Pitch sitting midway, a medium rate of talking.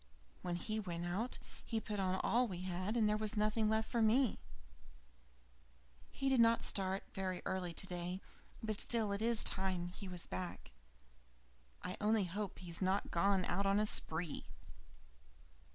No: high, 195 Hz; average, 155 wpm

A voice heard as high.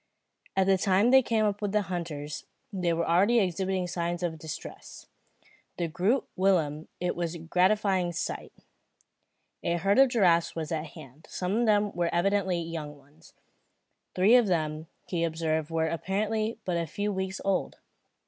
No: medium, 180 Hz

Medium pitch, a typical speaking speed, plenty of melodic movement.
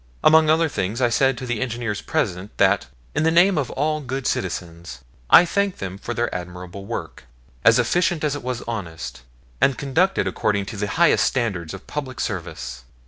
No: low, 120 Hz; average, 185 wpm; wide, 7.7 semitones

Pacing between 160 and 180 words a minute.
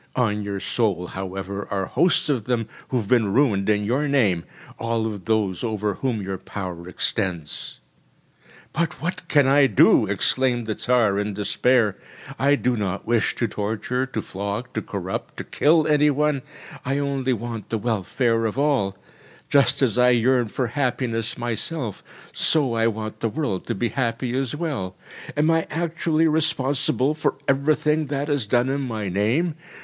Yes: average, 165 wpm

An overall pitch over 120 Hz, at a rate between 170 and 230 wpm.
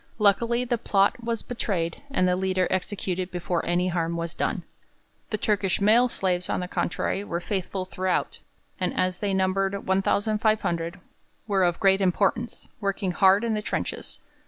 No: high, 190 Hz; average, 160 wpm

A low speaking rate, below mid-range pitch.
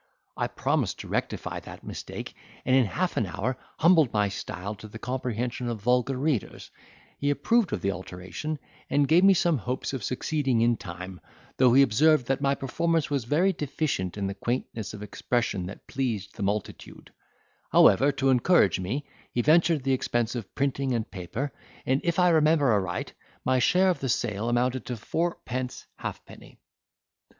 No: average, 170 wpm; low, 125 Hz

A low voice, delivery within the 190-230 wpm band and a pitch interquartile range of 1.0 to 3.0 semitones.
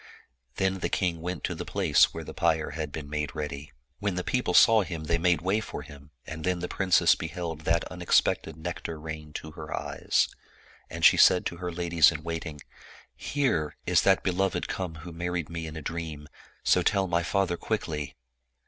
Yes: very low, 85 Hz; average, 195 wpm; narrow, 2.6 semitones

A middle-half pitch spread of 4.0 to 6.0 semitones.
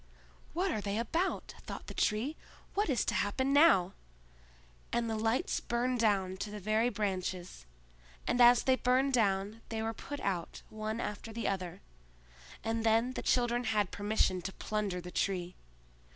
No: average, 3.6 semitones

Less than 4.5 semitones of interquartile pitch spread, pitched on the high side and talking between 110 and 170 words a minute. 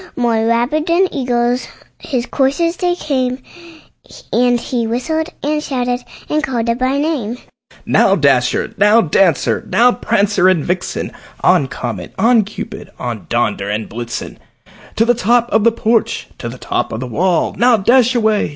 Yes: average, 4.0 semitones; high, 235 Hz; average, 160 wpm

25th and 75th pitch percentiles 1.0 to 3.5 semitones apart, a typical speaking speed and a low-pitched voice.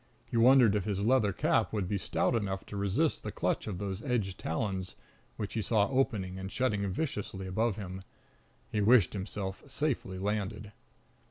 Yes: average, 2.8 semitones; average, 170 wpm; low, 100 Hz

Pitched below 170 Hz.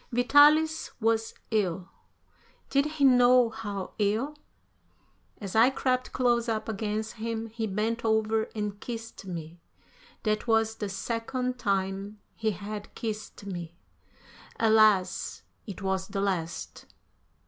No: high, 220 Hz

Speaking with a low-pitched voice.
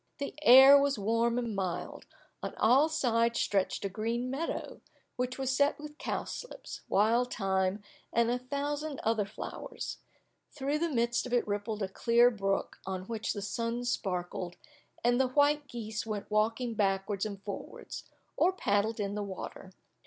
No: high, 230 Hz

